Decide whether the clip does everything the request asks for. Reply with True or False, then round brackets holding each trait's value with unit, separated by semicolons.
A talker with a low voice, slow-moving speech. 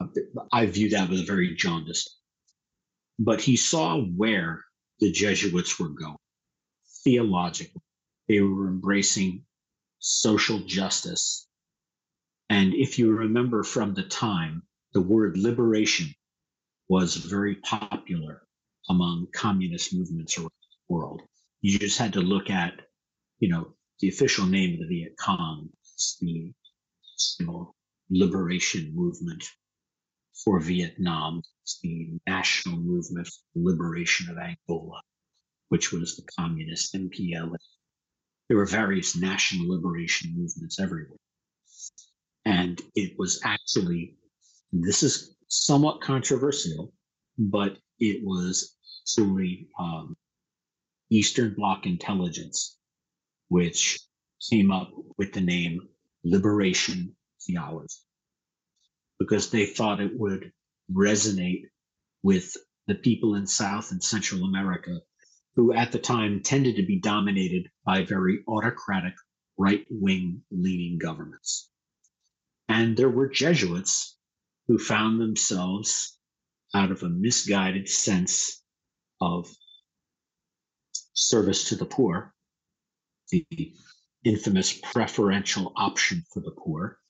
True (105 Hz; 105 wpm)